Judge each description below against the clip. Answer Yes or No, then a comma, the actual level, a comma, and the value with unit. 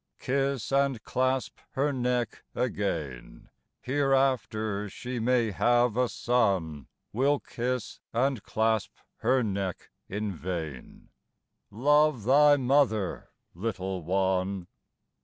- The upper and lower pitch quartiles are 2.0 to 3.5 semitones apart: No, average, 5.0 semitones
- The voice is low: Yes, low, 115 Hz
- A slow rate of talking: Yes, slow, 100 wpm